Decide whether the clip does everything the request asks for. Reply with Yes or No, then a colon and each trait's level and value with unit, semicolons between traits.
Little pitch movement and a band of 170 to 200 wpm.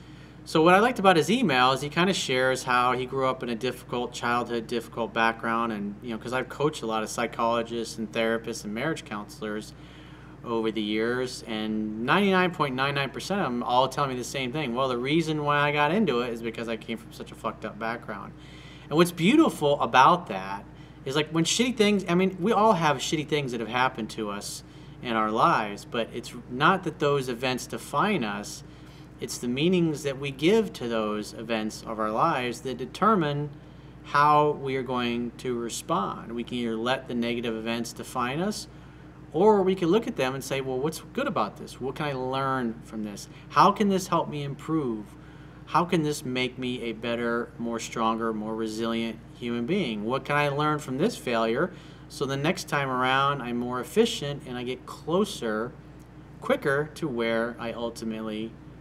No: average, 4.6 semitones; average, 195 wpm